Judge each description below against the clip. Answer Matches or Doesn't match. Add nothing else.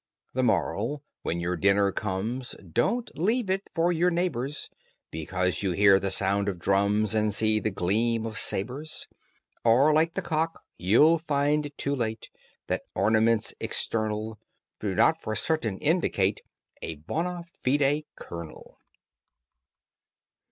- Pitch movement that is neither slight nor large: Doesn't match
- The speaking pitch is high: Doesn't match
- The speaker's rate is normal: Doesn't match